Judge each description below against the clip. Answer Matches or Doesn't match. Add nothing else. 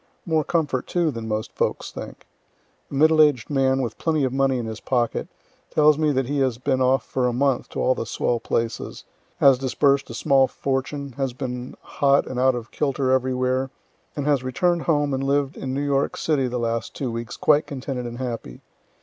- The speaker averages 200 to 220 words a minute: Matches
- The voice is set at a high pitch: Doesn't match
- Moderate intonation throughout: Doesn't match